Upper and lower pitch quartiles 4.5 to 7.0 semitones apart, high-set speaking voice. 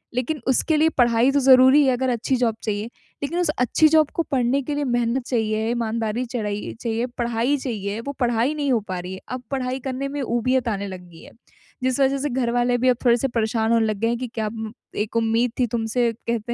No: average, 2.7 semitones; high, 240 Hz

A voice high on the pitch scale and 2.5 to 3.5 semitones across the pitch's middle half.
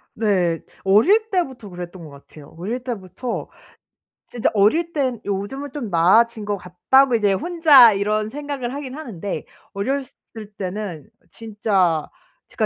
No: high, 215 Hz; wide, 5.6 semitones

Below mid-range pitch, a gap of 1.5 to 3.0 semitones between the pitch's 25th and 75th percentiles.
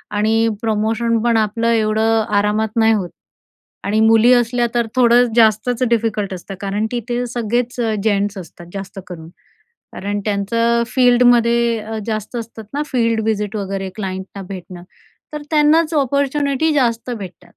No: high, 225 Hz; narrow, 2.6 semitones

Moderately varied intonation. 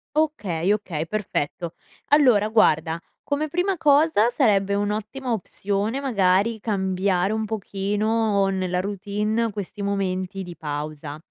Yes: average, 3.3 semitones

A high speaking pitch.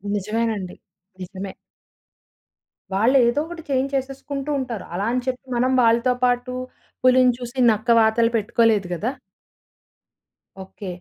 Yes: high, 235 Hz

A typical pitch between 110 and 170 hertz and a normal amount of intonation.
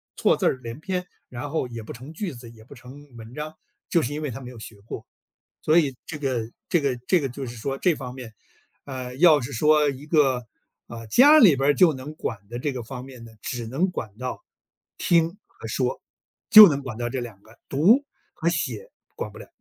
Yes: low, 135 Hz; average, 4.3 semitones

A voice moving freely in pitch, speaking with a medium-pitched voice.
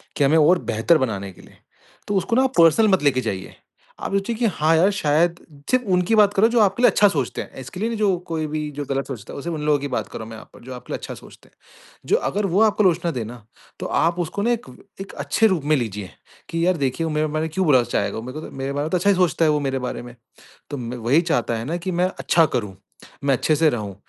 Yes: wide, 6.2 semitones; medium, 155 Hz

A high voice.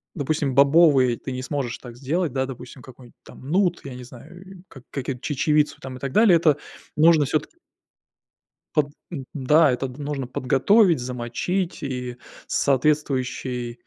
No: low, 135 Hz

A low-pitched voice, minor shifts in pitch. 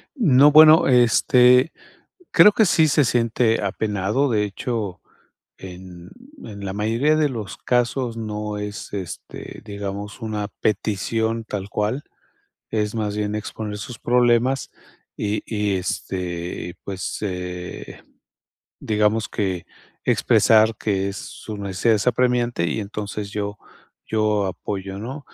No: low, 105 Hz; average, 3.0 semitones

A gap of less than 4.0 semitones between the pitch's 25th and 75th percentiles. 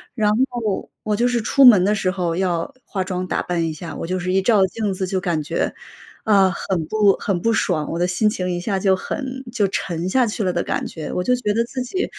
Yes: average, 3.5 semitones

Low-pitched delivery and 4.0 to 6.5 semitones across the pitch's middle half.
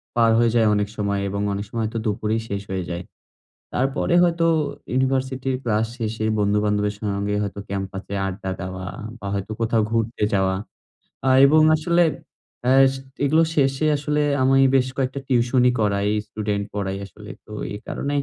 Yes: low, 110 Hz; average, 4.7 semitones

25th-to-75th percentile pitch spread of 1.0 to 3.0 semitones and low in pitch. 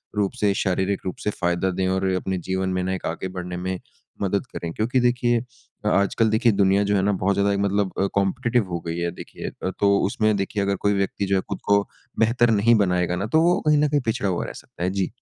Yes: narrow, 2.4 semitones; low, 100 Hz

